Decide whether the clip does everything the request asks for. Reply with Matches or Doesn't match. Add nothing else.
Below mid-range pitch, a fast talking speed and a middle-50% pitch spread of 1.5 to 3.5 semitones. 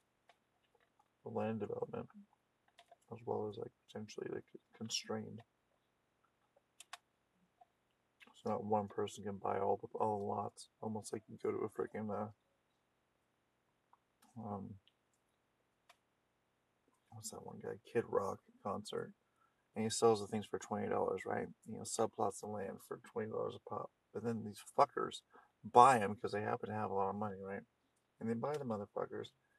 Doesn't match